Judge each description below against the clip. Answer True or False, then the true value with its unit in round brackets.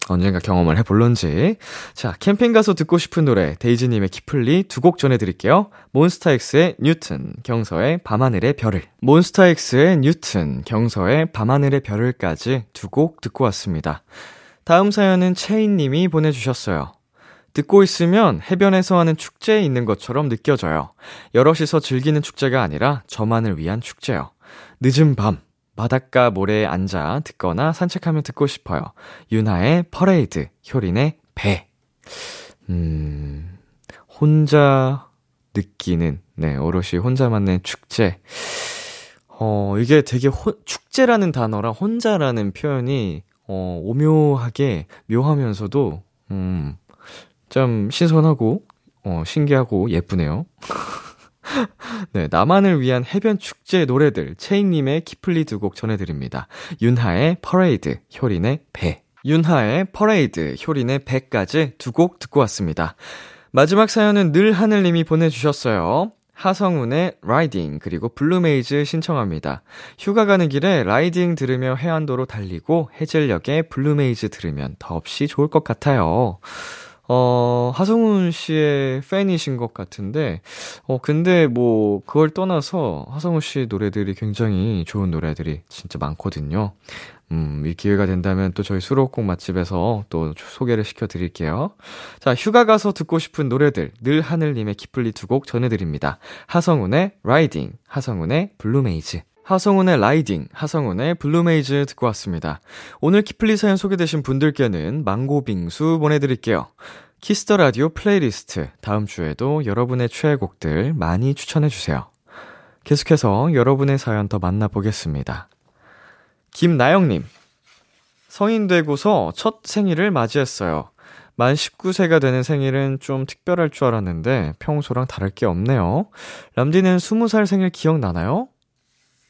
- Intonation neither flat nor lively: False (8.0 semitones)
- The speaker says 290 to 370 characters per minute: True (300 characters per minute)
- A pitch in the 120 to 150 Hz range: True (135 Hz)